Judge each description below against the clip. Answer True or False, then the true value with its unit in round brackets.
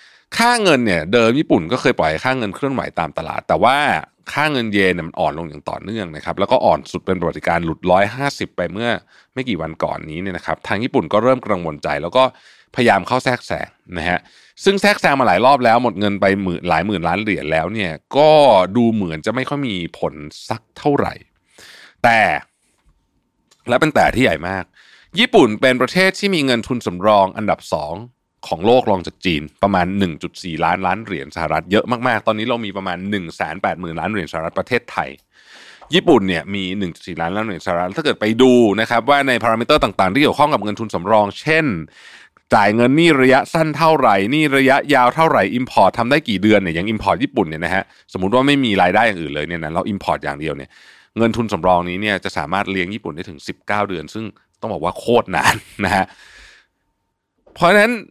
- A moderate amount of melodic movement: False (6.2 semitones)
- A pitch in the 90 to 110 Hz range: True (105 Hz)